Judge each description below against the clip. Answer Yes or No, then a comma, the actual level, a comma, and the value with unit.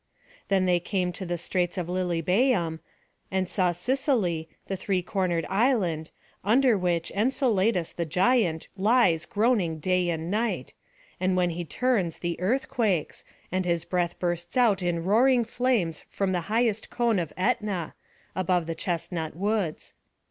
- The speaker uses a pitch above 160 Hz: Yes, medium, 185 Hz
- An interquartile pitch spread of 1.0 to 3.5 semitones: No, average, 4.2 semitones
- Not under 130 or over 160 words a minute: Yes, average, 150 wpm